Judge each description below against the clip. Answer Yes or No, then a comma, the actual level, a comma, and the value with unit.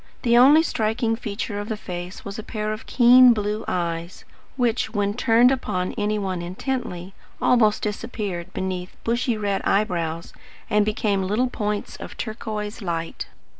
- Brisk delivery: No, average, 150 wpm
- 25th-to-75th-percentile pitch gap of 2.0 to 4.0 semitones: Yes, average, 3.7 semitones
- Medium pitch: No, high, 210 Hz